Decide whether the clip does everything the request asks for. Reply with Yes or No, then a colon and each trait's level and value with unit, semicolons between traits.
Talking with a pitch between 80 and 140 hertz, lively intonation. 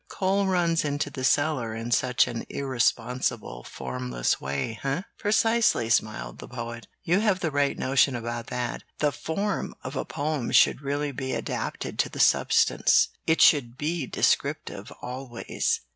No: low, 135 Hz; average, 4.8 semitones